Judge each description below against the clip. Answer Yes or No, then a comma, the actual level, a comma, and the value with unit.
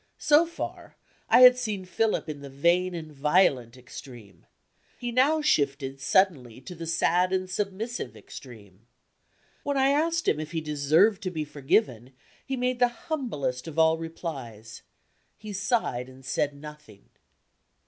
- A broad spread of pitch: Yes, wide, 8.3 semitones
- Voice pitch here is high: No, medium, 160 Hz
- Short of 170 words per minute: Yes, average, 150 wpm